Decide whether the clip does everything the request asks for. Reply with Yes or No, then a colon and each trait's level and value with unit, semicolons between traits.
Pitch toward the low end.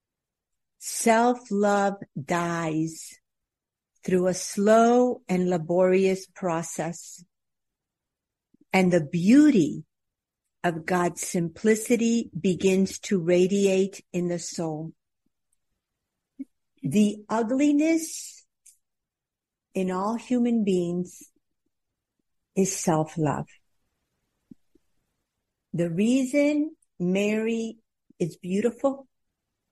No: high, 190 Hz